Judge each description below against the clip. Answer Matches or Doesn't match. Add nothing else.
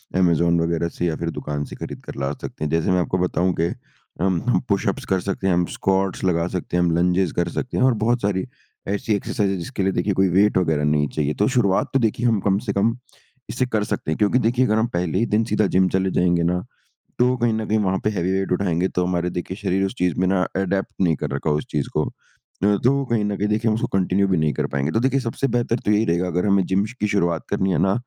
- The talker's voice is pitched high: Doesn't match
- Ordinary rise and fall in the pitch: Matches